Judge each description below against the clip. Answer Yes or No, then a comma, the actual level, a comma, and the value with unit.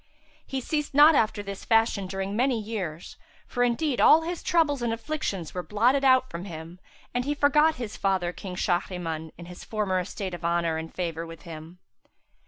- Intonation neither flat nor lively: No, wide, 6.8 semitones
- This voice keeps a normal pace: Yes, average, 185 wpm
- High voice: Yes, high, 200 Hz